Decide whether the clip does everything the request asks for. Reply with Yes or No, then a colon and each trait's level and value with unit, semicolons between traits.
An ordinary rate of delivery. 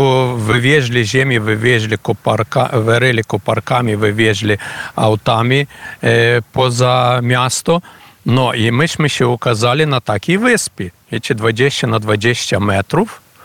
Yes: average, 120 wpm